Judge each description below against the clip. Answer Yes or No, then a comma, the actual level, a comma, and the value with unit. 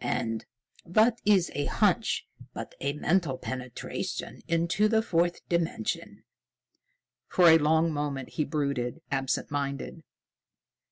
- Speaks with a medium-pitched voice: Yes, medium, 160 Hz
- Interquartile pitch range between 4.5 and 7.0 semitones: No, average, 3.8 semitones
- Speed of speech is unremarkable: No, slow, 115 wpm